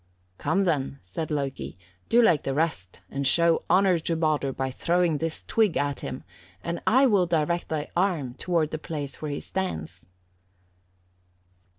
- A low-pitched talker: No, medium, 155 Hz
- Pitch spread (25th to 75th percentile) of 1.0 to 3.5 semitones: No, average, 3.9 semitones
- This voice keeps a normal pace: Yes, average, 160 wpm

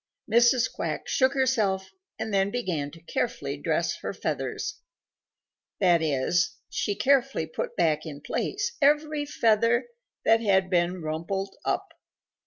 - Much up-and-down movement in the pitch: Yes, wide, 6.7 semitones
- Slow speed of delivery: Yes, slow, 130 wpm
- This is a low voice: No, high, 200 Hz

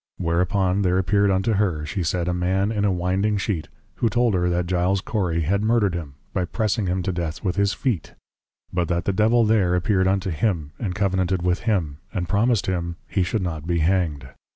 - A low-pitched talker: Yes, very low, 95 Hz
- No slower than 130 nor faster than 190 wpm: No, fast, 205 wpm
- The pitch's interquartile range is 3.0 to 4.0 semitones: No, narrow, 2.5 semitones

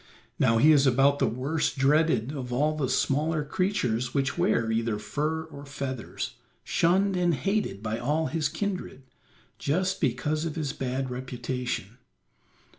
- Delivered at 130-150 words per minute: Yes, average, 145 wpm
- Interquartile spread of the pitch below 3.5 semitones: No, average, 4.1 semitones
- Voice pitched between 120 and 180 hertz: Yes, medium, 140 Hz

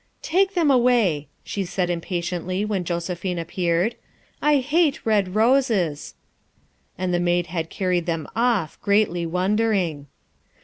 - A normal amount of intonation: Yes, average, 4.7 semitones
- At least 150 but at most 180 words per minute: No, average, 140 wpm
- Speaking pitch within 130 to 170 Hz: No, medium, 185 Hz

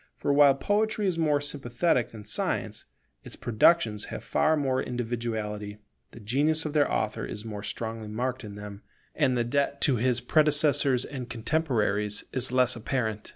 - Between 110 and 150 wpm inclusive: No, average, 160 wpm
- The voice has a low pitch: Yes, low, 125 Hz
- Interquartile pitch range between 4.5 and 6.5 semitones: Yes, average, 4.8 semitones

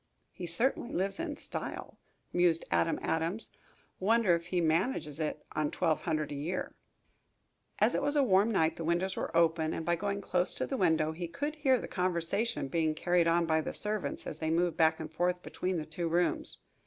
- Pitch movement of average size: Yes, average, 3.0 semitones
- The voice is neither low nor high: Yes, medium, 170 Hz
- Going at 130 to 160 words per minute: No, average, 200 wpm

